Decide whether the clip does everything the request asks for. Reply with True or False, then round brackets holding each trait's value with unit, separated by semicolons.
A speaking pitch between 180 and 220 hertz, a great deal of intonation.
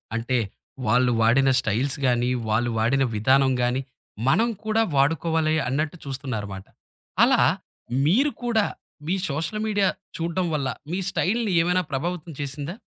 False (140 Hz; 6.0 semitones)